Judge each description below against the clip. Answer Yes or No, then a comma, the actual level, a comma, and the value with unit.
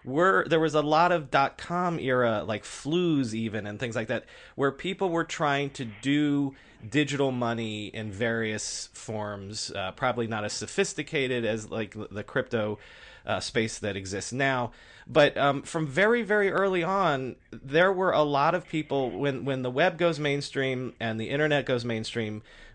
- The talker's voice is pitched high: No, low, 135 Hz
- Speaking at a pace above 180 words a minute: No, average, 170 wpm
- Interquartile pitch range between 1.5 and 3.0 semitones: No, wide, 5.6 semitones